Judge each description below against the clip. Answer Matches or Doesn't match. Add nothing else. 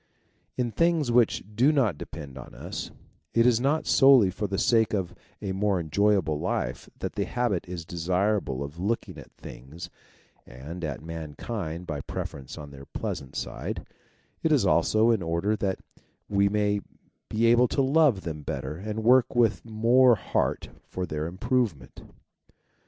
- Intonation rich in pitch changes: Matches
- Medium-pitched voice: Doesn't match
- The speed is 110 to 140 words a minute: Doesn't match